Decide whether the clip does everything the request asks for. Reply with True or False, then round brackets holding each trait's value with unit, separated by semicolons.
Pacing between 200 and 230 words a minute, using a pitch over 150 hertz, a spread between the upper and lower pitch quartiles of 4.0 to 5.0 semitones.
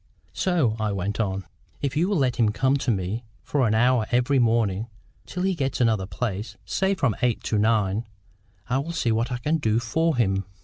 False (205 wpm; 120 Hz; 4.3 semitones)